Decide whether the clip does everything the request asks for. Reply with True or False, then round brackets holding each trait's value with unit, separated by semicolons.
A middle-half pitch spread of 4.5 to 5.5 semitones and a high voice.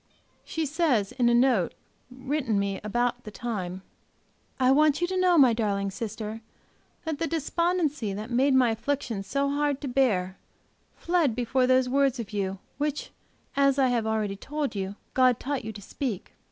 True (4.9 semitones; 250 Hz)